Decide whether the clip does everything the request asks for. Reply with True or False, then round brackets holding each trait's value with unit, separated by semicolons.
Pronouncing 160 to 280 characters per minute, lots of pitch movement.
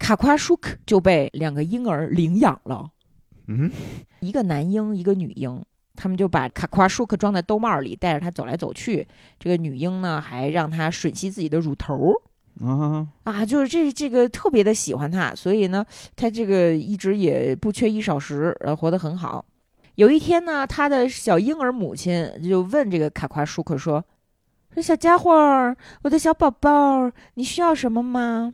True (260 characters per minute; 7.6 semitones)